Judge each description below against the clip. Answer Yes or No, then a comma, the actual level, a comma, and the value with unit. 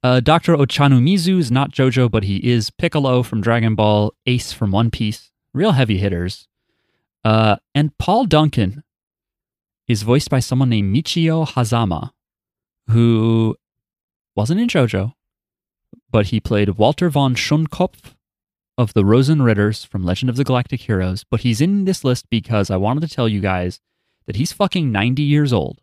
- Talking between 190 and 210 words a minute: No, average, 160 wpm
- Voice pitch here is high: No, low, 120 Hz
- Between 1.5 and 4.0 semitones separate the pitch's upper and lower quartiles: No, average, 4.8 semitones